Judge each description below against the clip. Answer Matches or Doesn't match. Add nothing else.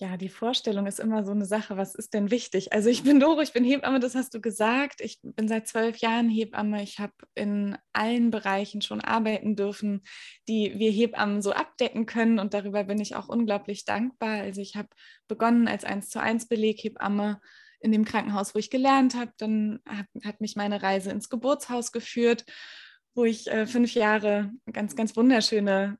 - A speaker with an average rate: Doesn't match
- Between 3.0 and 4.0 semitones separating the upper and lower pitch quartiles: Doesn't match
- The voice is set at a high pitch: Matches